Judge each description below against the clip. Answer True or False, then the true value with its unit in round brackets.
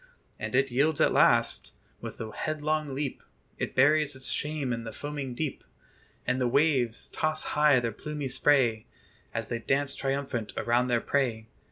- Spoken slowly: False (165 wpm)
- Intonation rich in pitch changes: False (3.5 semitones)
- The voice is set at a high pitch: False (135 Hz)